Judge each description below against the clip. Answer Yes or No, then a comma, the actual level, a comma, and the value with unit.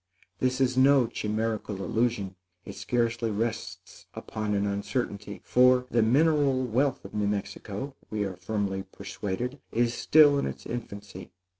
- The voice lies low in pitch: Yes, low, 115 Hz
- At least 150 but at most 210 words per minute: No, average, 140 wpm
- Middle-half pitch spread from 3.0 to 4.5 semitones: Yes, average, 3.9 semitones